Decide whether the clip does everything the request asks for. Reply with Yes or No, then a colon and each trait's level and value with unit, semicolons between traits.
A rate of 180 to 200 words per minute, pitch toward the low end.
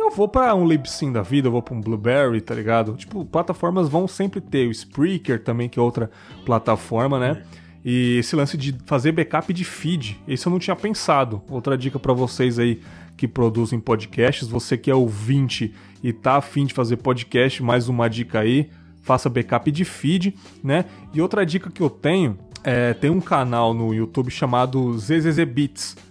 Yes: fast, 185 wpm; low, 130 Hz